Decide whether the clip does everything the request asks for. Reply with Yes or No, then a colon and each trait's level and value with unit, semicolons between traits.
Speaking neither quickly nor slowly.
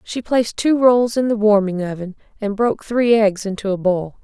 No: fast, 215 wpm